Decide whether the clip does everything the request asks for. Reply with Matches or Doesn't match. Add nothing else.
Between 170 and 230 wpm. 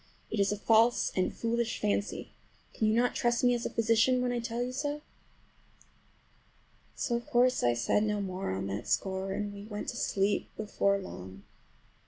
Matches